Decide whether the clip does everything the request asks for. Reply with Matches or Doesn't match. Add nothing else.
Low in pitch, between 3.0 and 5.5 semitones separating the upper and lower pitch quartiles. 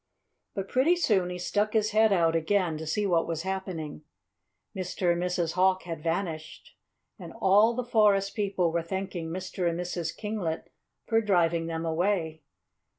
Doesn't match